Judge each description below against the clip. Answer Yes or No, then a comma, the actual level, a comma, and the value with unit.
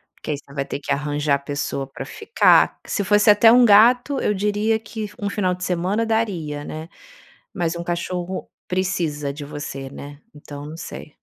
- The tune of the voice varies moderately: No, wide, 6.0 semitones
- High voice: No, medium, 175 Hz